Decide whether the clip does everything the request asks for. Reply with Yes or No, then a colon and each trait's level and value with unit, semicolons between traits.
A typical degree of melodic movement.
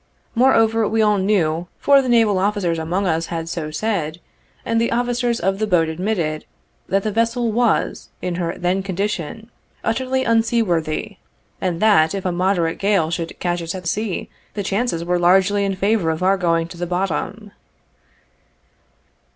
Yes: average, 4.5 semitones